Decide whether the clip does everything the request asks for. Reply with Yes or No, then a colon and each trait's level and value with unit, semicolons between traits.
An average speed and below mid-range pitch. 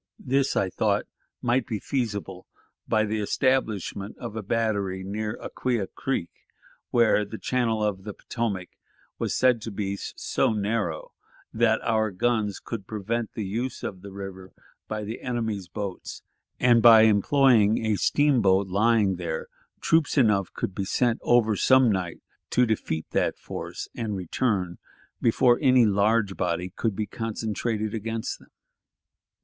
Yes: average, 145 wpm; low, 110 Hz